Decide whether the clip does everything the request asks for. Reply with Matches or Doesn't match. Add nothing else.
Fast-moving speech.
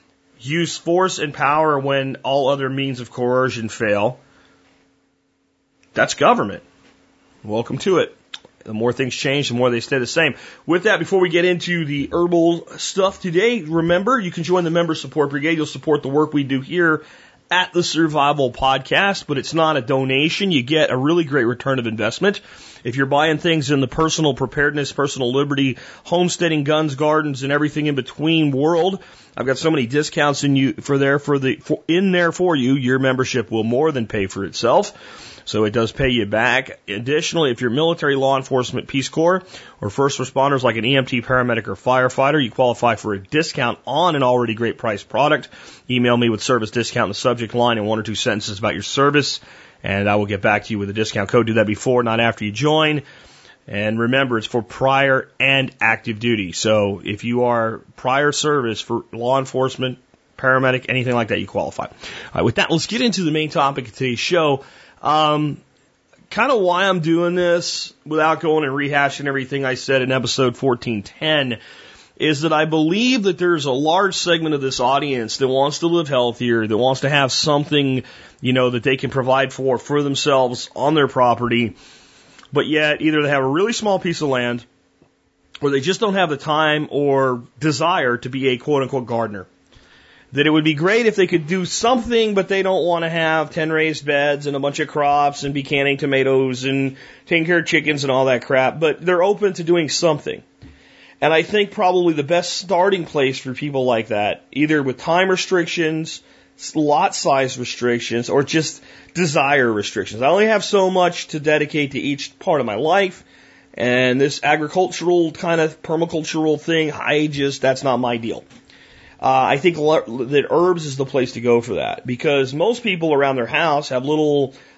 Doesn't match